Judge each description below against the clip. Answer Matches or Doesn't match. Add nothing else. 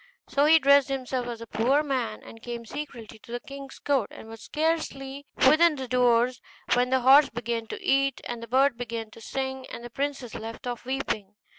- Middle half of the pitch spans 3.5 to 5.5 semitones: Doesn't match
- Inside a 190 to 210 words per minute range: Matches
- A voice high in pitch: Matches